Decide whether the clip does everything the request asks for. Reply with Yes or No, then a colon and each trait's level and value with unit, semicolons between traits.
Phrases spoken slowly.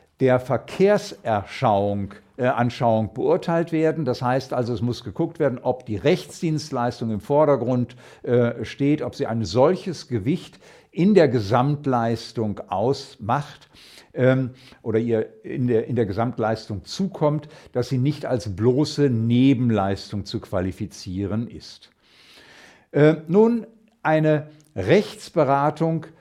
Yes: slow, 115 wpm